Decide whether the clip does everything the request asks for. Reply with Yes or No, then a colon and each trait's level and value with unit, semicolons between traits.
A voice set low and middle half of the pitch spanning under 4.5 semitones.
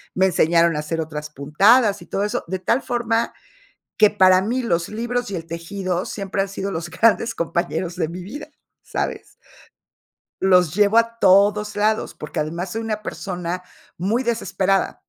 No: high, 190 Hz; average, 4.0 semitones